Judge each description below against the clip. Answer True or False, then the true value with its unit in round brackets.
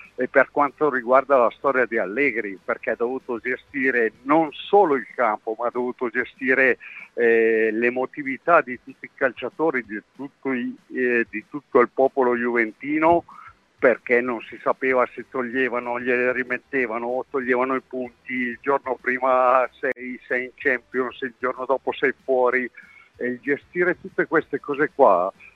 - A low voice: True (130 Hz)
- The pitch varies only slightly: True (1.8 semitones)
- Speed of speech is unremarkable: True (155 wpm)